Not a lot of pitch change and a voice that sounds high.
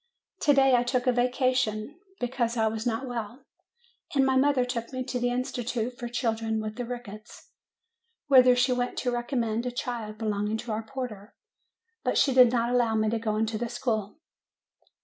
Yes: narrow, 2.3 semitones; high, 240 Hz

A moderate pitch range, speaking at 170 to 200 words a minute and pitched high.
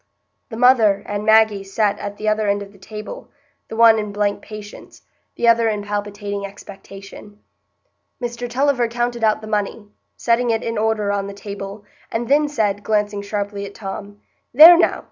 No: narrow, 2.2 semitones; average, 175 wpm; high, 210 Hz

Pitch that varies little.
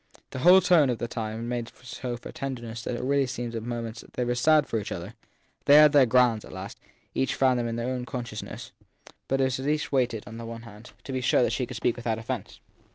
Yes: narrow, 2.3 semitones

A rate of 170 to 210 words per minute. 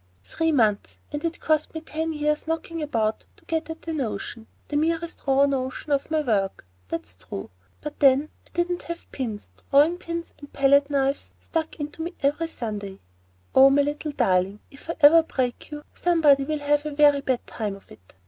Yes: average, 185 wpm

